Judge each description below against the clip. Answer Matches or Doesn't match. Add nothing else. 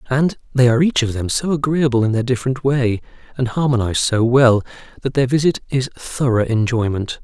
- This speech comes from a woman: Doesn't match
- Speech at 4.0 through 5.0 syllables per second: Doesn't match